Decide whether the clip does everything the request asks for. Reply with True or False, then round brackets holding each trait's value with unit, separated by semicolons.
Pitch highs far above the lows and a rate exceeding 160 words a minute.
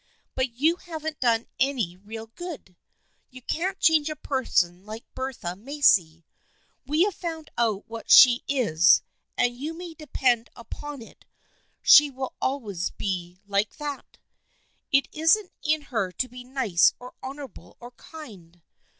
False (5.9 semitones; 140 wpm)